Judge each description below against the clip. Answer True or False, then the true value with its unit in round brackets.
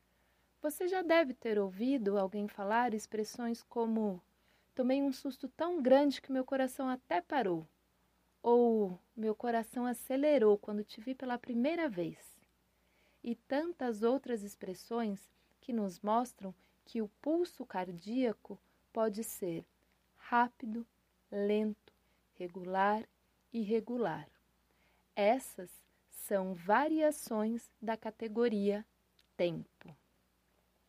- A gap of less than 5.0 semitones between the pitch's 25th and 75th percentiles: True (4.1 semitones)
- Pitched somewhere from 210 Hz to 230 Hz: True (225 Hz)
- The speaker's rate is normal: False (105 wpm)